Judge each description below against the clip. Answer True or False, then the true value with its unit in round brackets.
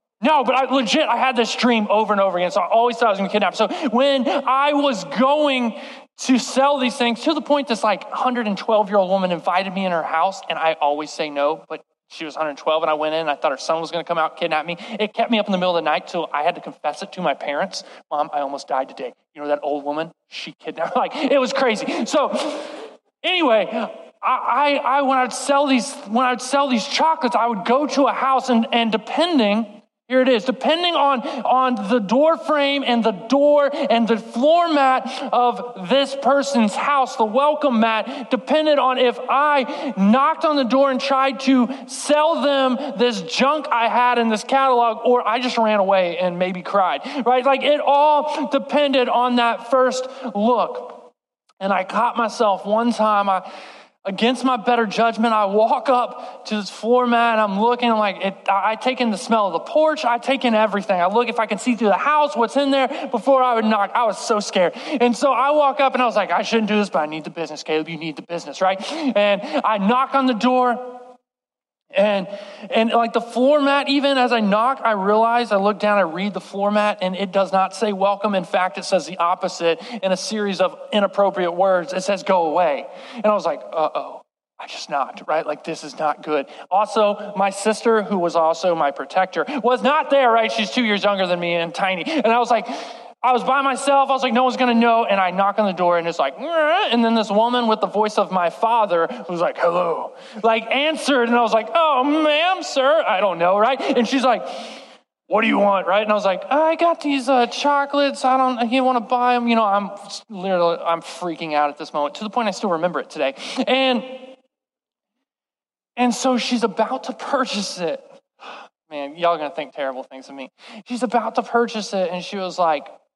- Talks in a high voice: True (235 Hz)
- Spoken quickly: True (230 wpm)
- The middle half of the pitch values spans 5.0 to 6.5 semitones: True (5.3 semitones)